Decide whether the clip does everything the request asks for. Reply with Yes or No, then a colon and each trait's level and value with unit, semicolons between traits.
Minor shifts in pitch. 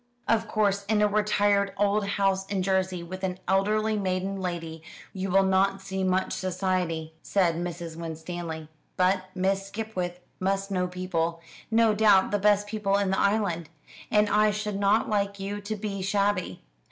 Yes: narrow, 2.0 semitones